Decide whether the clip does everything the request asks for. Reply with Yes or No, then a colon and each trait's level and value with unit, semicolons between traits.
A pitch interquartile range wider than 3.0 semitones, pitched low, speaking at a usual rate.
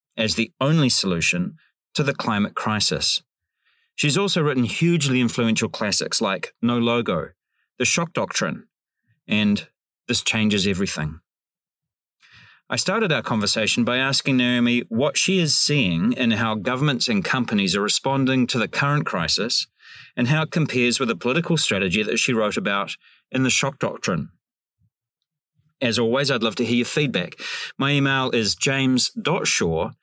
Yes: average, 4.5 semitones; low, 125 Hz; average, 150 wpm